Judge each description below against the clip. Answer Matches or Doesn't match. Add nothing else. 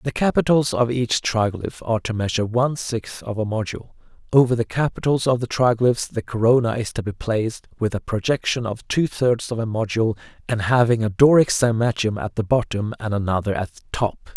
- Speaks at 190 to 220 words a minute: Matches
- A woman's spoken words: Doesn't match